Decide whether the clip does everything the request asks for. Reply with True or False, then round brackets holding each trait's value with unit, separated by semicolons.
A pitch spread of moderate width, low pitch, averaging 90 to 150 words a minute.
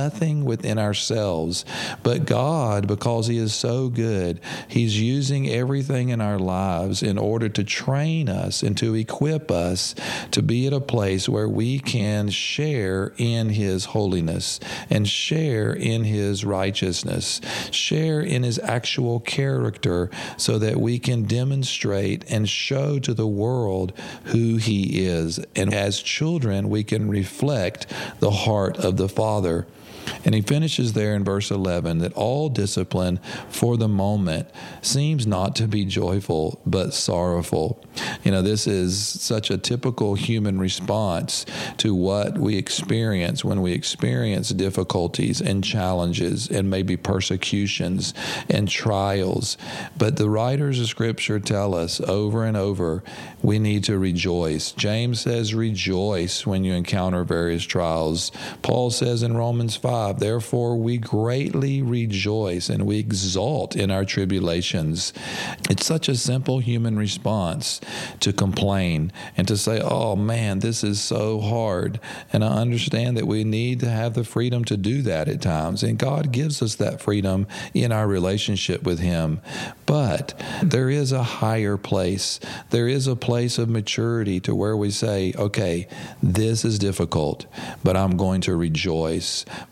True (3.8 semitones; 105 Hz; 145 wpm)